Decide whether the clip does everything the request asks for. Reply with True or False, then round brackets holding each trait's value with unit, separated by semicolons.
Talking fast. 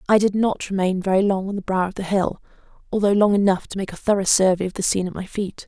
True (275 wpm)